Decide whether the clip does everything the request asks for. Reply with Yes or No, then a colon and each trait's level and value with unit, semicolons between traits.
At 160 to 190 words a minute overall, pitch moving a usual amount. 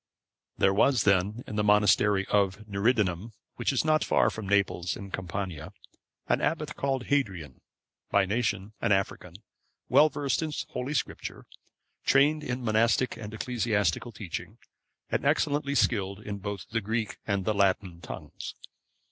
No: average, 140 wpm; average, 4.2 semitones